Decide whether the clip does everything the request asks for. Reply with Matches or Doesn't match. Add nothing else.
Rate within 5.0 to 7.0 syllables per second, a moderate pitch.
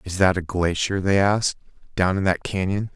Doesn't match